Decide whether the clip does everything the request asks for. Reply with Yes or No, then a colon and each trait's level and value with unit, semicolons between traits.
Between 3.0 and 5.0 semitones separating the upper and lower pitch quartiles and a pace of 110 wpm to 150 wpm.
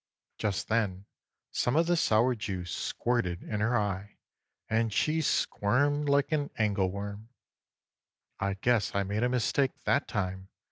Yes: average, 4.2 semitones; average, 145 wpm